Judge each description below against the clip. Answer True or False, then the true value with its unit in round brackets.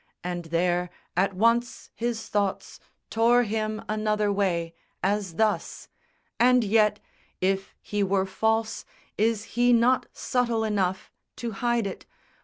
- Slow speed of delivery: True (125 wpm)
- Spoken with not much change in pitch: False (3.0 semitones)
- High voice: True (210 Hz)